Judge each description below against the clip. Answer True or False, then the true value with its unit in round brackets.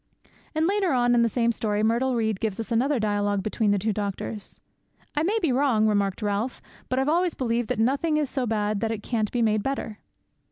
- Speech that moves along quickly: True (225 wpm)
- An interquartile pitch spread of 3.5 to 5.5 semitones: True (3.8 semitones)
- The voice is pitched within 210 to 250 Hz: True (230 Hz)